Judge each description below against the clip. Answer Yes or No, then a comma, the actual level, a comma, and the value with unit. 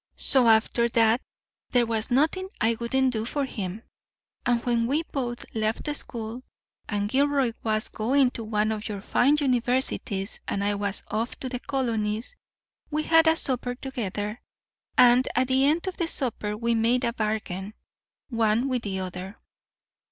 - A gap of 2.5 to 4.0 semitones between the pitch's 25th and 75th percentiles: Yes, average, 3.5 semitones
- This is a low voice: No, high, 235 Hz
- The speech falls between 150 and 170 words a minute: Yes, average, 160 wpm